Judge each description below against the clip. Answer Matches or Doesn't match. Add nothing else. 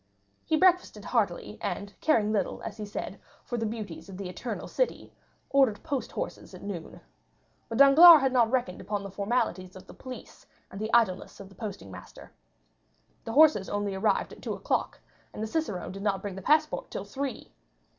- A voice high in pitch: Matches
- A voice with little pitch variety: Doesn't match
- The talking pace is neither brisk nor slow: Matches